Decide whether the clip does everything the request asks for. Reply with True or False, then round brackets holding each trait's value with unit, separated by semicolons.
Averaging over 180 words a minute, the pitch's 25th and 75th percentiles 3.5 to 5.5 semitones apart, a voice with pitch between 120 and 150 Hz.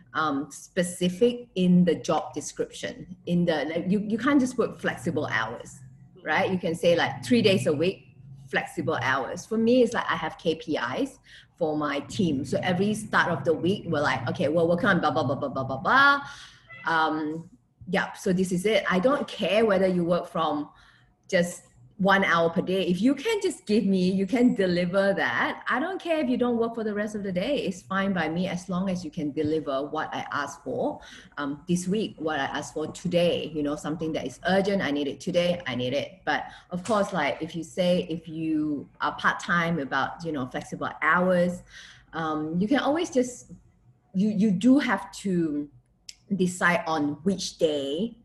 False (200 wpm; 4.2 semitones; 175 Hz)